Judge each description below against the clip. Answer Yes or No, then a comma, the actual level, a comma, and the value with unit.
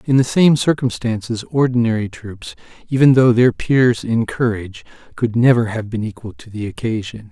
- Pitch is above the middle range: No, low, 115 Hz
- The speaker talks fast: No, average, 165 wpm